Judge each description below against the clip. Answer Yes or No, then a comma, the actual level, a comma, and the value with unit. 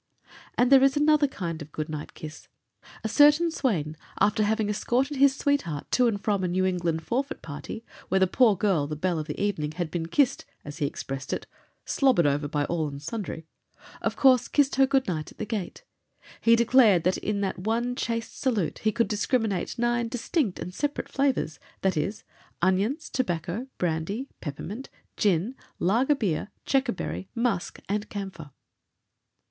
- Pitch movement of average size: No, wide, 7.0 semitones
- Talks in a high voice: Yes, high, 205 Hz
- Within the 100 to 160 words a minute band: No, average, 170 wpm